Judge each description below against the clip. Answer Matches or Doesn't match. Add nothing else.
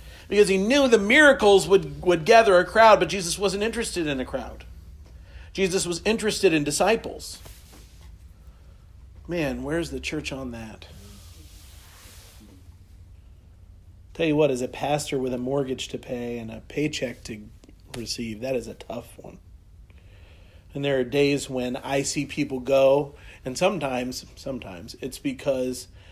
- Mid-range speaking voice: Doesn't match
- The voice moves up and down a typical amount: Doesn't match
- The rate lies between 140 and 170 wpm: Matches